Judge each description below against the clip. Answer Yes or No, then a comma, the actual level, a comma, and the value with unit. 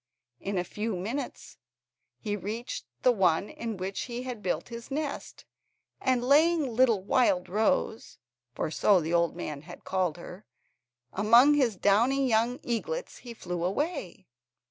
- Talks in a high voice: Yes, high, 220 Hz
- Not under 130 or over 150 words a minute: Yes, average, 145 wpm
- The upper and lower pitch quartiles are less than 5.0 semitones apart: No, wide, 5.4 semitones